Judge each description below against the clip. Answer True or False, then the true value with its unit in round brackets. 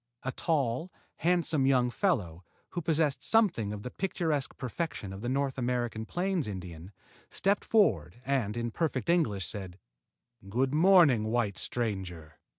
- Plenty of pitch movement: True (7.7 semitones)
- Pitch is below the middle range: True (125 Hz)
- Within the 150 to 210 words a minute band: False (140 wpm)